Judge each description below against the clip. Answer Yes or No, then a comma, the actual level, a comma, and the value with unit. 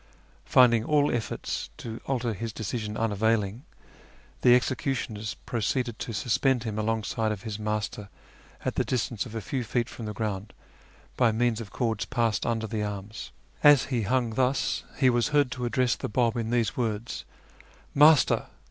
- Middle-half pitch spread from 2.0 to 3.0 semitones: Yes, narrow, 2.6 semitones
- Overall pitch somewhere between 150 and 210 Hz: No, low, 115 Hz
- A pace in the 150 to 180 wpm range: Yes, average, 165 wpm